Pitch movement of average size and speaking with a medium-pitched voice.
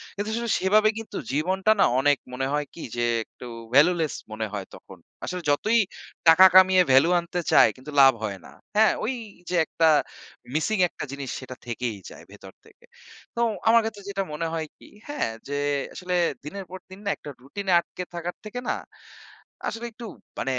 No: wide, 6.3 semitones; medium, 175 Hz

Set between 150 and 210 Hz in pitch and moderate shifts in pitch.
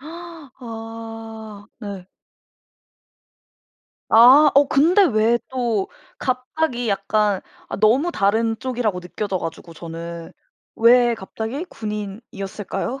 No: high, 225 Hz; average, 4.0 semitones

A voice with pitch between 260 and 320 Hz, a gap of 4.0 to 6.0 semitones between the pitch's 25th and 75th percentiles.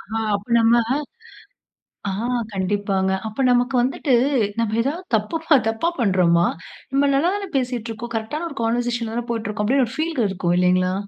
No: high, 230 Hz; average, 4.7 semitones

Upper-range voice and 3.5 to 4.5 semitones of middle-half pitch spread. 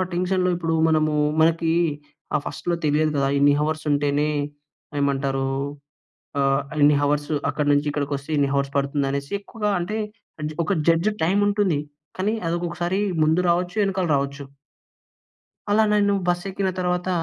No: medium, 160 Hz; average, 4.2 semitones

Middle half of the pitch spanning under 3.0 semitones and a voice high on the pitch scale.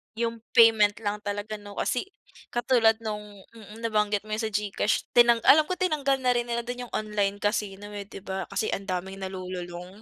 Yes: narrow, 2.4 semitones; high, 210 Hz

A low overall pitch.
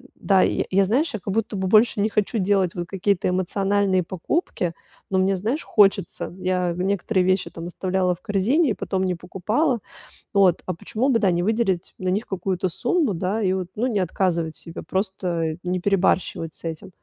No: high, 190 Hz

